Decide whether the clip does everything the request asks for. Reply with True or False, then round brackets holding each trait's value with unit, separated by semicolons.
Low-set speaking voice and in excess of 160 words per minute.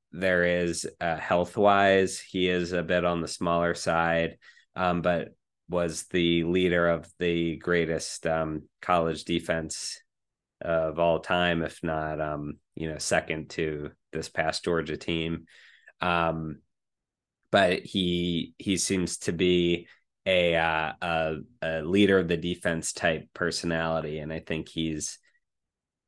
False (85 Hz; 135 wpm)